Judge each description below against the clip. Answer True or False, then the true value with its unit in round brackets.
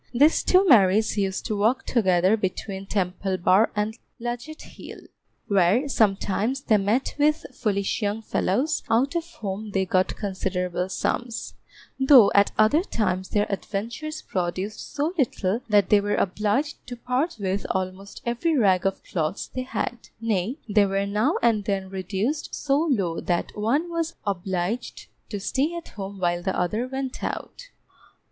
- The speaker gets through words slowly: False (155 wpm)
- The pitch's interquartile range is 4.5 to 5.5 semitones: True (4.8 semitones)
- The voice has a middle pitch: False (210 Hz)